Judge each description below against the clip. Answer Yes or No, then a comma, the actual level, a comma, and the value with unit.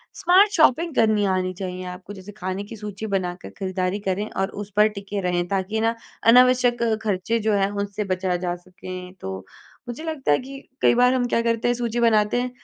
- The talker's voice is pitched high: Yes, high, 205 Hz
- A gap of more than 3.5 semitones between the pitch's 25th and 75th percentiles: Yes, average, 4.1 semitones